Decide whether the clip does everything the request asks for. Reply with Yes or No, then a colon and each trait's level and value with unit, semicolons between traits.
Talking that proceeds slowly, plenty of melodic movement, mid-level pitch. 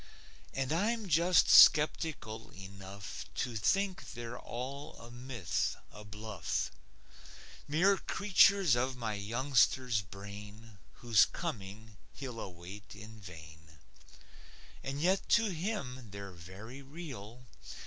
No: slow, 105 wpm; wide, 6.4 semitones; low, 120 Hz